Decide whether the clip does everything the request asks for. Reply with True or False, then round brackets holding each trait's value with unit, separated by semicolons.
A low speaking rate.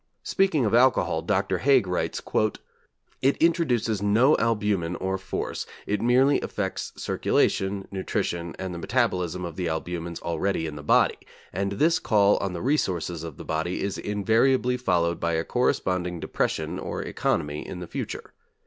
False (155 wpm)